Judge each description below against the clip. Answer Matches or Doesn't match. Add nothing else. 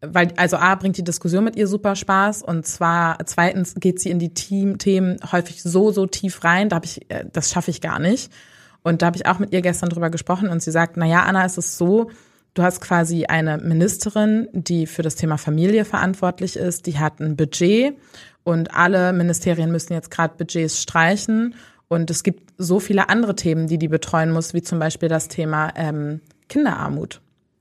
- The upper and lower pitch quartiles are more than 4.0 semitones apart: Doesn't match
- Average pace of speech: Doesn't match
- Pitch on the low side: Doesn't match